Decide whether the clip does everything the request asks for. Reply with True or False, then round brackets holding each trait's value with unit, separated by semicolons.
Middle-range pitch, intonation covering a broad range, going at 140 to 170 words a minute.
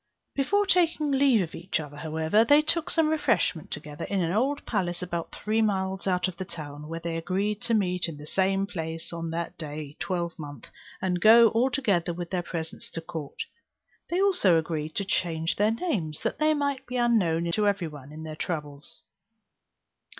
False (180 Hz; 5.7 semitones; 185 wpm)